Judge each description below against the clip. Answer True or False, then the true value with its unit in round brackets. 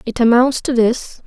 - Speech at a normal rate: True (190 wpm)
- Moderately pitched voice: False (240 Hz)